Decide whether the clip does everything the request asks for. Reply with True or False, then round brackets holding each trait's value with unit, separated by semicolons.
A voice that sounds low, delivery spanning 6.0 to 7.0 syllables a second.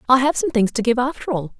False (240 Hz; 6.5 syllables/s)